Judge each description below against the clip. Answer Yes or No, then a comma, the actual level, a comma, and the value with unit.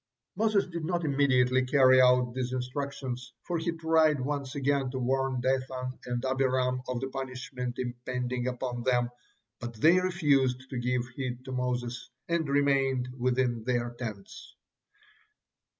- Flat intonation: Yes, narrow, 1.9 semitones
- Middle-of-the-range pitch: No, low, 130 Hz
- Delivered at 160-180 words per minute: No, average, 145 wpm